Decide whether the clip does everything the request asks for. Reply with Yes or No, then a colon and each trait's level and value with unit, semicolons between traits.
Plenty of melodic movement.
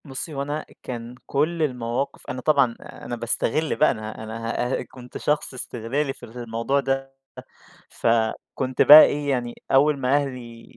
No: average, 3.2 semitones